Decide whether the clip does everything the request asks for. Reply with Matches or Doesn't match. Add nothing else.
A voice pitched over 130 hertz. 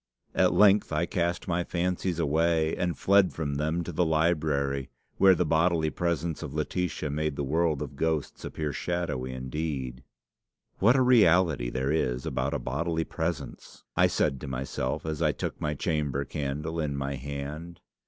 Doesn't match